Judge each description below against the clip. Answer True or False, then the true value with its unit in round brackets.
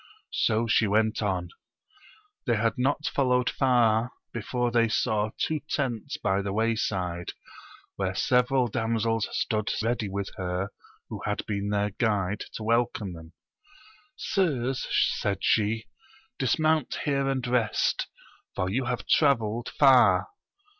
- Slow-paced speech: True (125 wpm)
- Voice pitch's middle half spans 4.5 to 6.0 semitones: False (3.5 semitones)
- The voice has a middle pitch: False (115 Hz)